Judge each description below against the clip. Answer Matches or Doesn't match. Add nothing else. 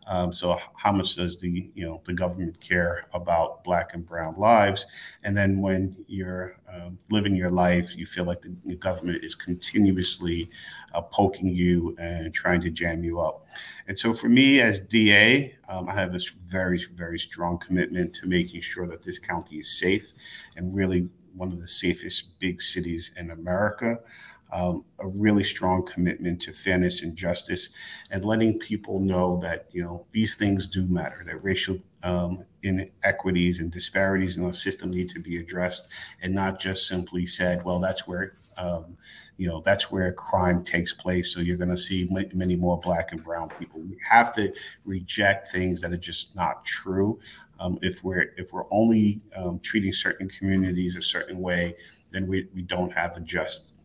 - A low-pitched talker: Matches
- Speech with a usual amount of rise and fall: Doesn't match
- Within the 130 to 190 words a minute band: Matches